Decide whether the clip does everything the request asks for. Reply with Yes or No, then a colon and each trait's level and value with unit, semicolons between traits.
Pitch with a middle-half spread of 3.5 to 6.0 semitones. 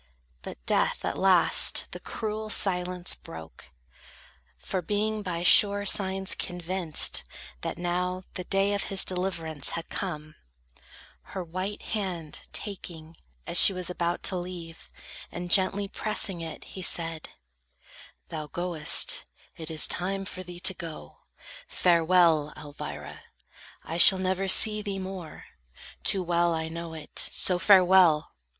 No: average, 2.7 semitones